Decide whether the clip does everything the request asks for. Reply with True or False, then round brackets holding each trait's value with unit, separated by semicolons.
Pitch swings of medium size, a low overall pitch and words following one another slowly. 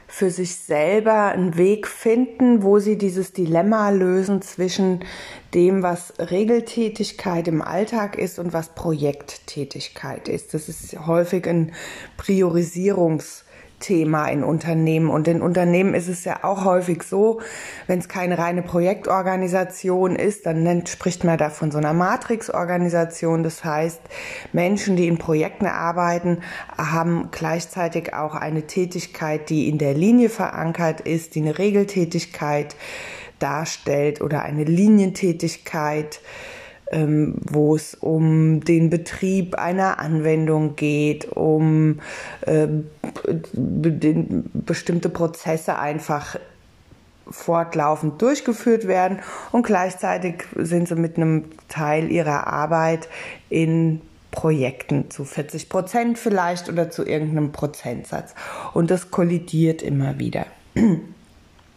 False (3.1 semitones; 170 Hz; 120 wpm)